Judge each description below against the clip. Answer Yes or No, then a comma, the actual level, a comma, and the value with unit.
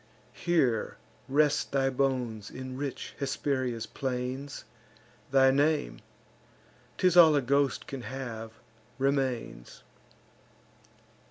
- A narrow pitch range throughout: Yes, narrow, 2.1 semitones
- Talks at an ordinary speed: No, slow, 90 wpm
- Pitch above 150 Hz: No, low, 135 Hz